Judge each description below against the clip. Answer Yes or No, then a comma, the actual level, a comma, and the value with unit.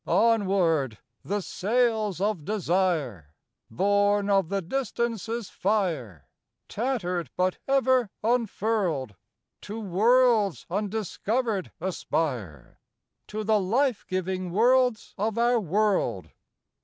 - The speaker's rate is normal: No, slow, 95 wpm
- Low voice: No, high, 200 Hz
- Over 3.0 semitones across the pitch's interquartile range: Yes, average, 4.1 semitones